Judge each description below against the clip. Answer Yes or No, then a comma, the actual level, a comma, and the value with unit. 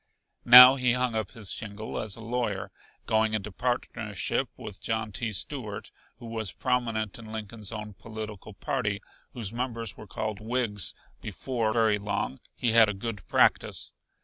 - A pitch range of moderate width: No, narrow, 2.2 semitones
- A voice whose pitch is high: No, low, 110 Hz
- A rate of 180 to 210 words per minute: No, average, 155 wpm